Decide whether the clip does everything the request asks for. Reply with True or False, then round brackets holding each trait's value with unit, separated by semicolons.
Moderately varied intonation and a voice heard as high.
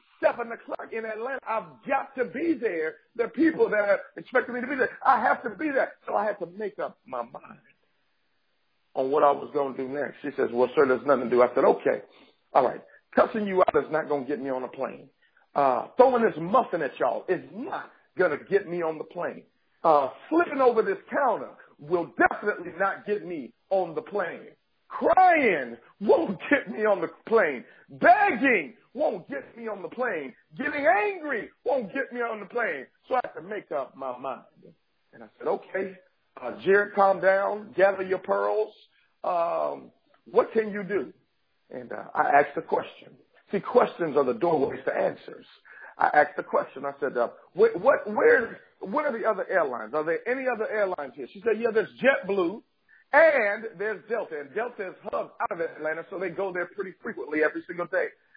False (7.1 semitones; 215 Hz)